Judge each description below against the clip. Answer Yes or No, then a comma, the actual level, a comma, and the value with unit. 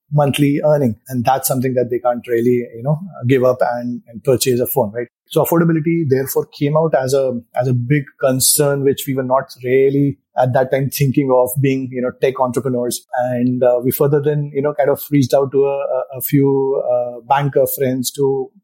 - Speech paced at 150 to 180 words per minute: No, fast, 205 wpm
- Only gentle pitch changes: Yes, narrow, 2.3 semitones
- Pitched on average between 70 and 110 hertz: No, low, 135 Hz